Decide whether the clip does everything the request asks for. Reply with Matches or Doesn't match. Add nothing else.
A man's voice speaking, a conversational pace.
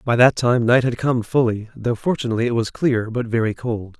Doesn't match